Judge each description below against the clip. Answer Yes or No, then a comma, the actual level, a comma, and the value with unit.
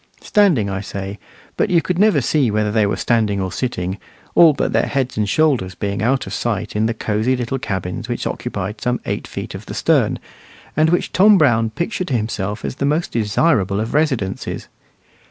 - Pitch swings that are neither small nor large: No, wide, 5.9 semitones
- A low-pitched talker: Yes, low, 115 Hz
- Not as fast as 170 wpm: No, average, 195 wpm